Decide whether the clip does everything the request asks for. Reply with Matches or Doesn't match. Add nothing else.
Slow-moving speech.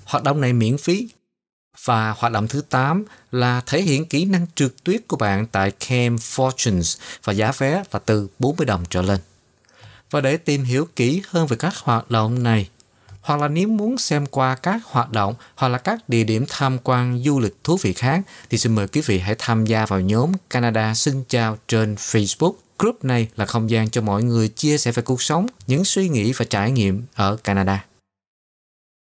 Doesn't match